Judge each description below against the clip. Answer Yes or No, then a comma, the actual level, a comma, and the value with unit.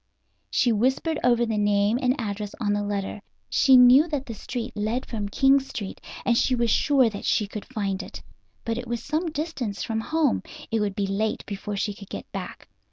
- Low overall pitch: No, high, 225 Hz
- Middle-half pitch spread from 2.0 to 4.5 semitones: Yes, average, 3.8 semitones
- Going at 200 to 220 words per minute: Yes, fast, 205 wpm